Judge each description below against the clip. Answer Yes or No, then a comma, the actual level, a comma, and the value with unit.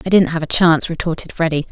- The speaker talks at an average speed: No, fast, 245 wpm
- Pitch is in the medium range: Yes, medium, 165 Hz